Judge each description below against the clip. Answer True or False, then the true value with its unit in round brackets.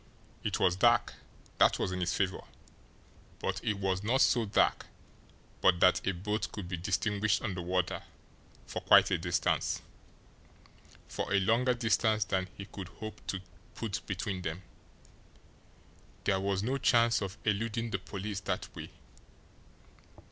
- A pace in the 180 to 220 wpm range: False (150 wpm)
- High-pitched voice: False (100 Hz)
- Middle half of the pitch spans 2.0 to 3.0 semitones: True (2.7 semitones)